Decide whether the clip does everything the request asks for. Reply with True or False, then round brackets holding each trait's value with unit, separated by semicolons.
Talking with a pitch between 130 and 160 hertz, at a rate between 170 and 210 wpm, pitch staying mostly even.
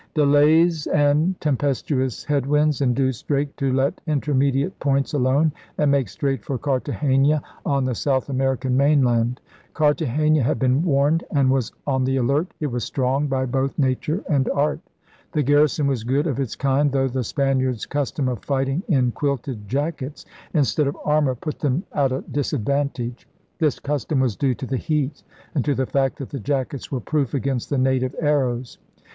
True (140 Hz; 175 wpm; 2.1 semitones)